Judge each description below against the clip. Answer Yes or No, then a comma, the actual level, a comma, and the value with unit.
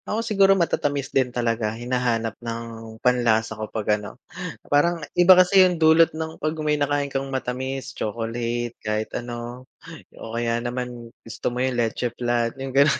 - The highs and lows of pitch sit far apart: No, average, 3.7 semitones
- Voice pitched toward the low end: Yes, low, 125 Hz